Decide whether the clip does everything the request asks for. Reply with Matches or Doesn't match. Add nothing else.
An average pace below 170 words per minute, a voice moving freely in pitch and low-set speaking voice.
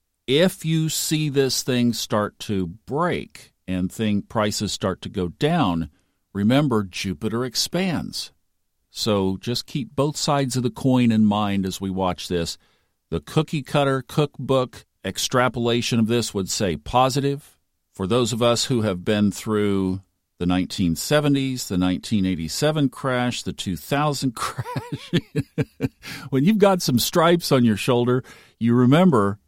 Matches